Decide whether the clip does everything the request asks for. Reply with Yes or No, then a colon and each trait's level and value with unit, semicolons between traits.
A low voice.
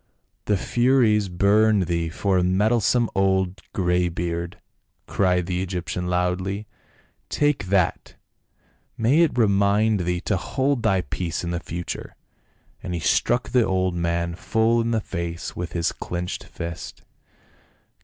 Yes: very low, 95 Hz